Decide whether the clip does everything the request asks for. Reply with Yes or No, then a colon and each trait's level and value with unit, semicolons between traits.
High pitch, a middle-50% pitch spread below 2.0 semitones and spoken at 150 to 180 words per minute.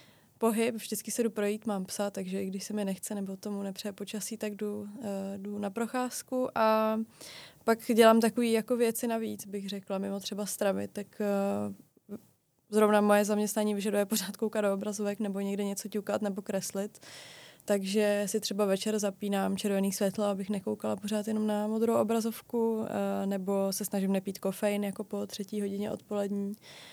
Yes: high, 205 Hz; narrow, 1.5 semitones; average, 165 wpm